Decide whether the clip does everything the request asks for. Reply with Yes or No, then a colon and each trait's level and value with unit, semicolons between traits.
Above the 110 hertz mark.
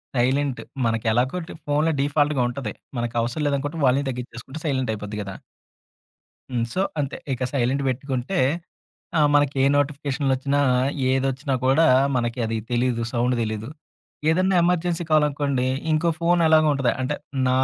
Yes: low, 135 Hz